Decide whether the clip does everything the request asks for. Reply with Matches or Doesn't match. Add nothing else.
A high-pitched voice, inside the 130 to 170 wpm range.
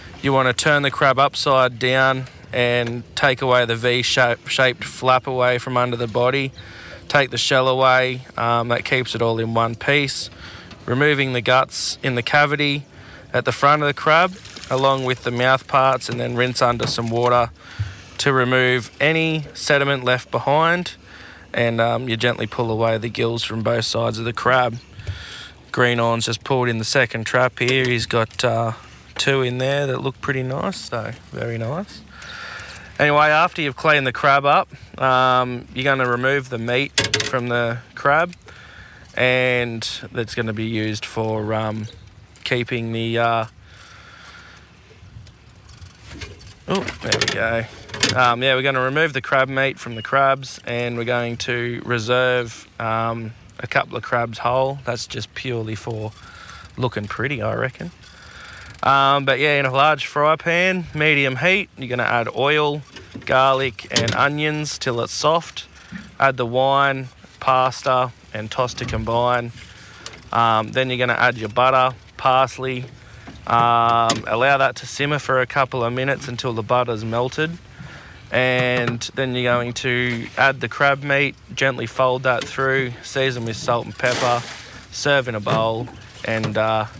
Doesn't match